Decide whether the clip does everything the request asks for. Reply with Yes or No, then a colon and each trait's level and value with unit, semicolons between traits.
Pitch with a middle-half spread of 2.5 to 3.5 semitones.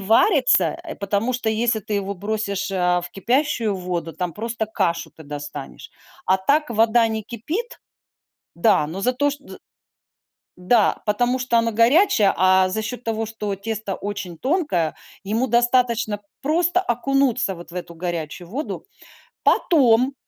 No: average, 4.7 semitones